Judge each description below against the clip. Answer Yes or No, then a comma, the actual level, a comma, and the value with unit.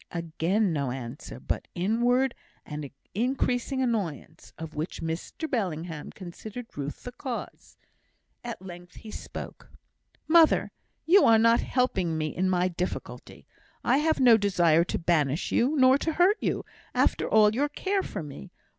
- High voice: Yes, high, 200 Hz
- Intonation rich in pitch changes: Yes, wide, 7.5 semitones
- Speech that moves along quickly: No, average, 145 wpm